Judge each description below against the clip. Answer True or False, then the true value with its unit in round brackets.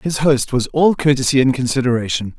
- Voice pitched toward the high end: False (135 Hz)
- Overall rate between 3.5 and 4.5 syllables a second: False (5.5 syllables/s)